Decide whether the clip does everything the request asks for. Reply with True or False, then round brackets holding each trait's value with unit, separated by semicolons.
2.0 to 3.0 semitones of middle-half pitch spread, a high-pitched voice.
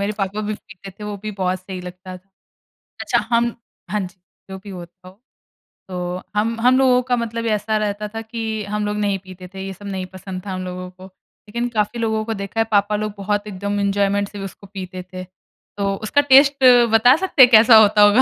True (2.7 semitones; 205 Hz)